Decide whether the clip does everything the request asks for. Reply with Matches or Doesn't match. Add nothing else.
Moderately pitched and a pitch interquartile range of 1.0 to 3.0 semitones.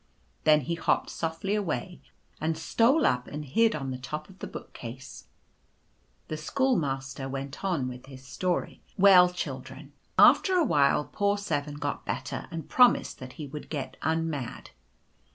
Doesn't match